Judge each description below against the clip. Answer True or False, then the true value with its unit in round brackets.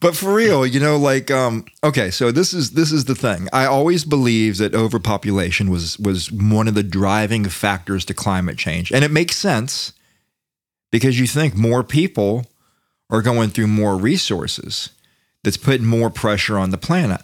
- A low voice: True (115 Hz)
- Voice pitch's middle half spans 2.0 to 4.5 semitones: False (5.2 semitones)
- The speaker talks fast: False (180 wpm)